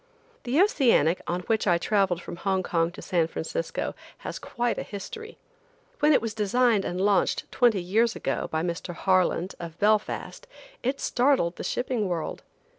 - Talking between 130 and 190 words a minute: Yes, average, 165 wpm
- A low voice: No, high, 205 Hz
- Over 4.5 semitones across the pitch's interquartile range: Yes, wide, 5.6 semitones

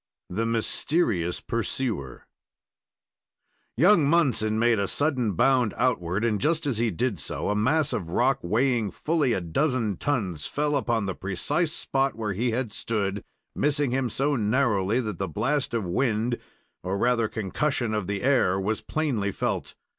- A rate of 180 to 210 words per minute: No, average, 155 wpm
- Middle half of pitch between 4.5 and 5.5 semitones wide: Yes, average, 5.1 semitones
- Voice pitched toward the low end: Yes, low, 115 Hz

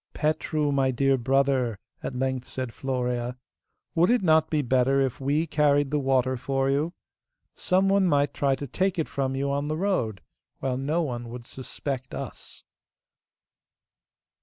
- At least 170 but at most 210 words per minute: No, average, 160 wpm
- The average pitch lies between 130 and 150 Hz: Yes, low, 135 Hz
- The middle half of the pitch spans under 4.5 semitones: Yes, average, 2.7 semitones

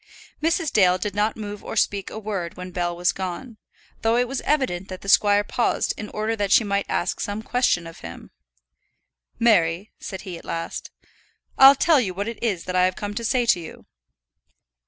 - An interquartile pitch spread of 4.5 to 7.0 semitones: No, average, 3.9 semitones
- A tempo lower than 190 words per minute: No, average, 200 wpm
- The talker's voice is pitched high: Yes, high, 205 Hz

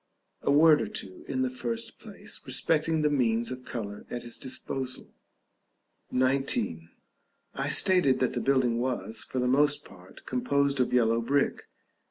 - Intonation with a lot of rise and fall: No, average, 3.2 semitones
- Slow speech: No, average, 160 wpm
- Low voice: Yes, low, 130 Hz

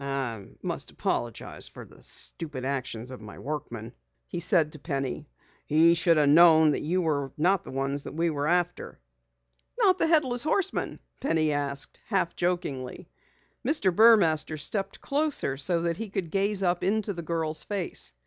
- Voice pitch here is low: No, medium, 165 Hz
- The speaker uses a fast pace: No, average, 160 wpm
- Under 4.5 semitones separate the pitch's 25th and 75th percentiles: No, average, 5.3 semitones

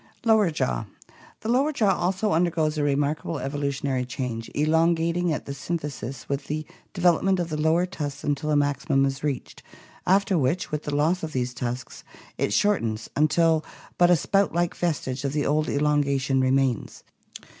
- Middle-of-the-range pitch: Yes, medium, 150 Hz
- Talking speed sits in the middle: Yes, average, 170 wpm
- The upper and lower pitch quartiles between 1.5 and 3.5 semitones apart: No, average, 3.9 semitones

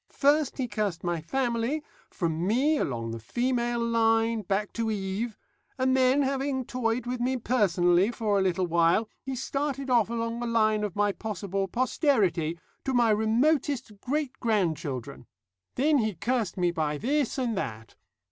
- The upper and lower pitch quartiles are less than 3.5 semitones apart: No, average, 5.1 semitones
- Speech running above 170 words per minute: No, average, 155 wpm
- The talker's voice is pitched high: Yes, high, 225 Hz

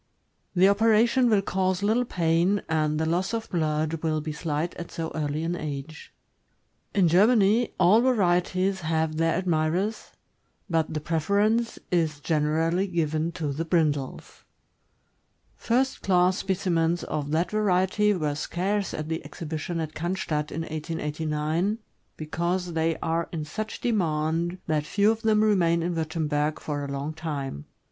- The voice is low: No, medium, 165 Hz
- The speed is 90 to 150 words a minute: Yes, average, 145 wpm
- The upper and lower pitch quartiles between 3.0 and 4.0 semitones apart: Yes, average, 3.5 semitones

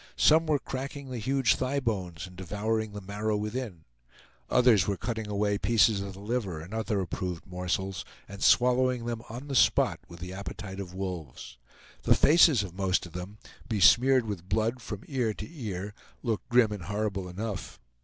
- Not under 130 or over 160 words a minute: No, average, 175 wpm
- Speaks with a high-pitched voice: No, low, 105 Hz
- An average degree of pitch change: Yes, average, 4.1 semitones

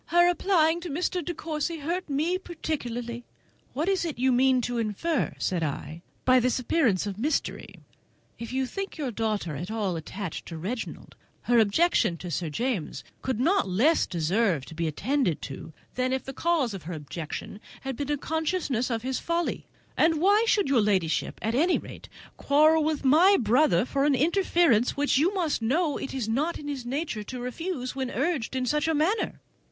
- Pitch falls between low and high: No, very high, 265 Hz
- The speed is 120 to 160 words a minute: No, average, 190 wpm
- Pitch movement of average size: No, wide, 6.7 semitones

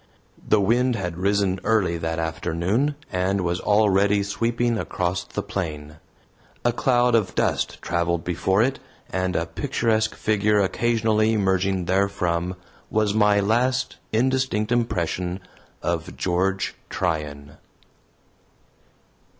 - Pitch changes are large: No, average, 4.0 semitones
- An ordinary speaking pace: No, slow, 110 wpm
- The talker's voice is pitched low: Yes, low, 100 Hz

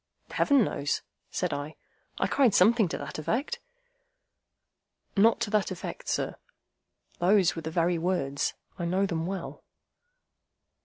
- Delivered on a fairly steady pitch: No, average, 4.3 semitones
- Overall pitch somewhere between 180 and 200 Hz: Yes, medium, 185 Hz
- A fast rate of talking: No, slow, 135 wpm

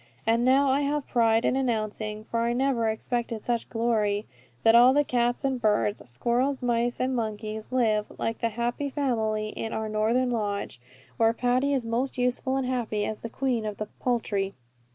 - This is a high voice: Yes, high, 235 Hz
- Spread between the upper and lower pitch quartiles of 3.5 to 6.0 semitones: No, average, 2.7 semitones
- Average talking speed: Yes, average, 180 wpm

